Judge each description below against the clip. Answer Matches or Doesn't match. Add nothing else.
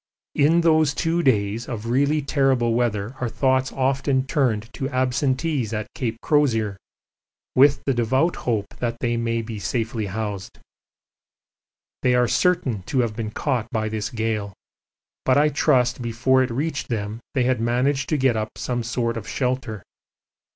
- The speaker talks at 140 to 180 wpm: Matches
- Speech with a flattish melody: Doesn't match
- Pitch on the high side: Doesn't match